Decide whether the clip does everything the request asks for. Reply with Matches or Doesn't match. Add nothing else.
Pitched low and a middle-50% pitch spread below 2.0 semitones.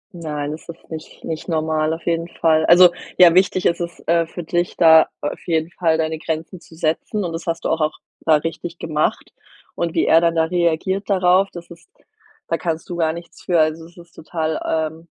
Doesn't match